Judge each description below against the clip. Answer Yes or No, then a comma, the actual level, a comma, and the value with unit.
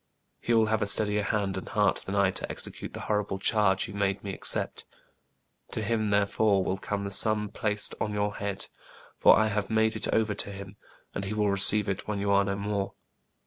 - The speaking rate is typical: No, fast, 215 wpm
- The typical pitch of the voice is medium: No, low, 105 Hz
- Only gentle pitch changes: Yes, narrow, 1.4 semitones